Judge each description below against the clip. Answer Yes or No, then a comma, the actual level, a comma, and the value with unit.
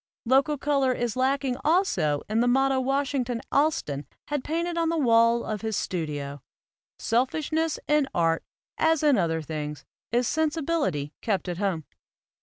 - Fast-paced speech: No, average, 150 wpm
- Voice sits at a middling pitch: No, very high, 250 Hz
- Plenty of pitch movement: Yes, wide, 8.8 semitones